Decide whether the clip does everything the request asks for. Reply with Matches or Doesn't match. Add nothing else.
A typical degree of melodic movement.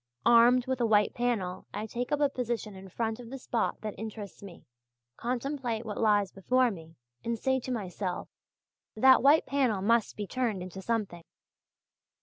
Matches